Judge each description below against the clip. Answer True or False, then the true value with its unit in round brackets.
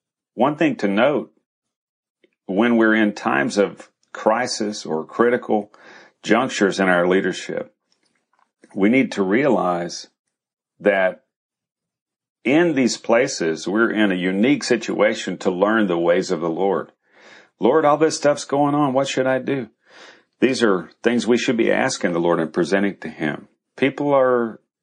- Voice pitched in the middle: False (105 Hz)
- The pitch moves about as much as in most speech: False (5.8 semitones)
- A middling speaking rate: True (145 wpm)